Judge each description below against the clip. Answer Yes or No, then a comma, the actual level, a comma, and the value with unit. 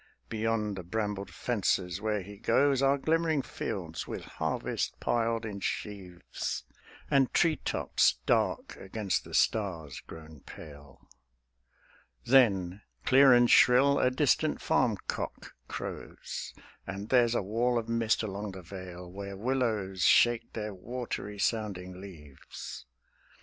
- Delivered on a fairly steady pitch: No, average, 4.2 semitones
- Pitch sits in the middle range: No, low, 105 Hz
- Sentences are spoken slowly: Yes, slow, 125 wpm